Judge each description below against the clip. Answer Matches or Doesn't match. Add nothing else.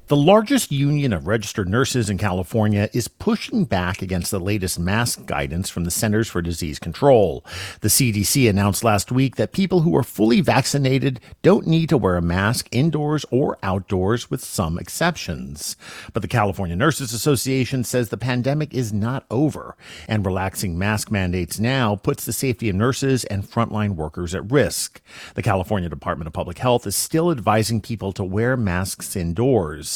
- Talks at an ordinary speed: Matches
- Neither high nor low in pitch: Doesn't match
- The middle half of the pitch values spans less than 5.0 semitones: Doesn't match